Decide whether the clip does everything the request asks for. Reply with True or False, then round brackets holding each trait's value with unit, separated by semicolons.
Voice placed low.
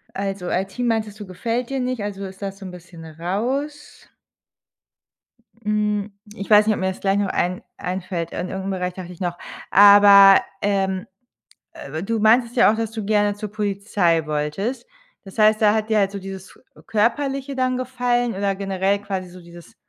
False (200 Hz)